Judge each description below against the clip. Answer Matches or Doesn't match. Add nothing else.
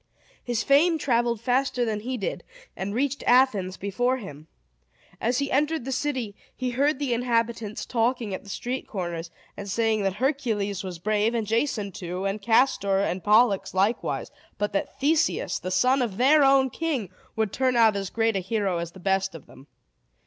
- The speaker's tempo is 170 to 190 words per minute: Matches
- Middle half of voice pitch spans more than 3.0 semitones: Matches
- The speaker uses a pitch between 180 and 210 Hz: Doesn't match